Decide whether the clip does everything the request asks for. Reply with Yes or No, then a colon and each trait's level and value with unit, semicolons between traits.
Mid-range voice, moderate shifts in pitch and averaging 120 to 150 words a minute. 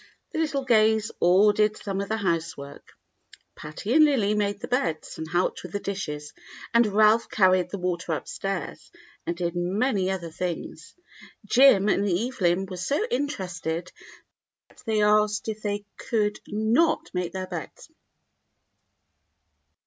No: high, 200 Hz; average, 3.6 semitones; average, 140 wpm